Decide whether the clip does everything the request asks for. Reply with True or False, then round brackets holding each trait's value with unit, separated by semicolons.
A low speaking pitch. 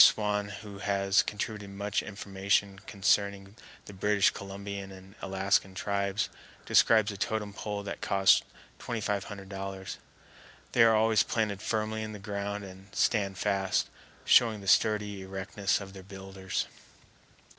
True (100 Hz)